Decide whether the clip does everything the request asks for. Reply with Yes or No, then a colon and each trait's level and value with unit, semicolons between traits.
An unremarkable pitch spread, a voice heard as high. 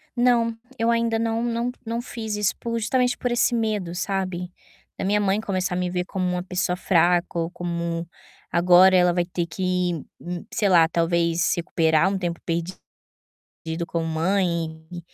No: average, 3.8 semitones; medium, 180 Hz